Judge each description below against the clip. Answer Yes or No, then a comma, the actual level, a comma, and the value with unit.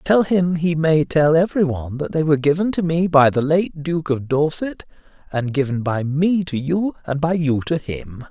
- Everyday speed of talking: No, fast, 215 wpm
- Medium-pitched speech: Yes, medium, 155 Hz